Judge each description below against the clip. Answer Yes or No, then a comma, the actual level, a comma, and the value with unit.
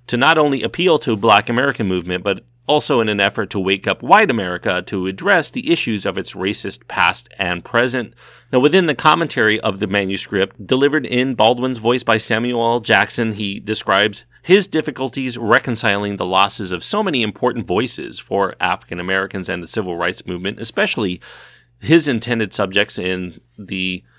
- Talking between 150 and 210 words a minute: Yes, average, 170 wpm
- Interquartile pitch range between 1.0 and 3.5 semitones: No, average, 4.4 semitones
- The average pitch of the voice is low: Yes, low, 110 Hz